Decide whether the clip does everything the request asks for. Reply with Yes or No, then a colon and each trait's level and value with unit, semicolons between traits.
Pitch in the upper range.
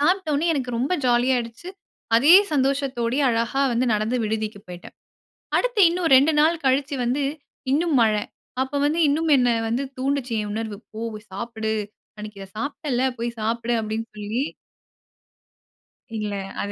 Yes: high, 245 Hz